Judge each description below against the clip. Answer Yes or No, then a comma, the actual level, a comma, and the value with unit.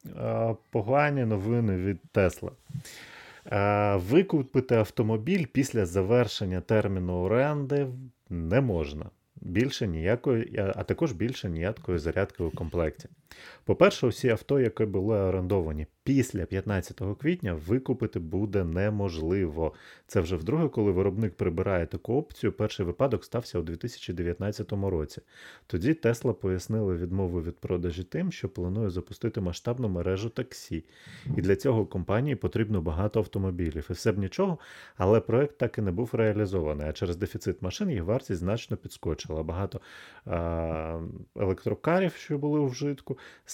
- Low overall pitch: Yes, low, 105 Hz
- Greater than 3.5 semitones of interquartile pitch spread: Yes, average, 5.1 semitones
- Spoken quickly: No, average, 130 wpm